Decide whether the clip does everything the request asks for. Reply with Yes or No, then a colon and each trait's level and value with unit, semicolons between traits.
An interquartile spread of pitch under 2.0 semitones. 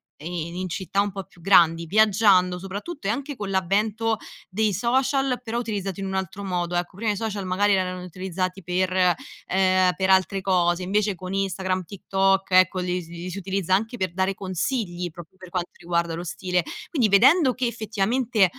No: narrow, 2.5 semitones